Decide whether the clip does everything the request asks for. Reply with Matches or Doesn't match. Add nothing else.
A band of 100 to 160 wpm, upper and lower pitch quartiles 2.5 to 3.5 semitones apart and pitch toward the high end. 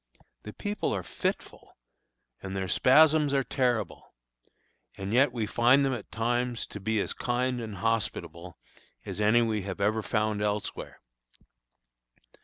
Doesn't match